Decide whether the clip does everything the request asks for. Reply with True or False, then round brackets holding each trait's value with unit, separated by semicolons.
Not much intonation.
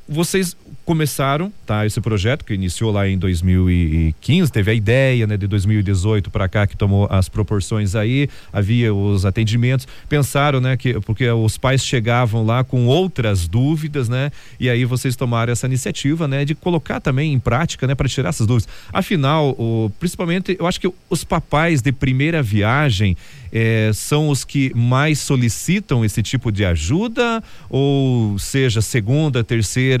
False (5.0 semitones)